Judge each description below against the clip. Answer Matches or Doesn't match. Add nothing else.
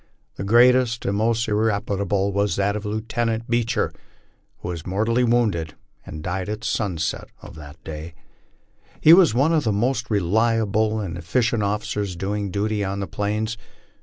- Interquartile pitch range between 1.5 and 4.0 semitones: Matches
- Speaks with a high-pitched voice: Doesn't match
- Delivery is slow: Doesn't match